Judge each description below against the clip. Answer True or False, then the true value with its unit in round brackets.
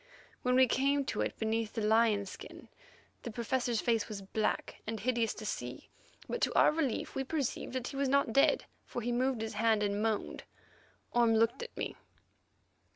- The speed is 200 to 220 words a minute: False (185 wpm)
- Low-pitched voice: False (230 Hz)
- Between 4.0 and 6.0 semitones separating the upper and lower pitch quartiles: False (2.9 semitones)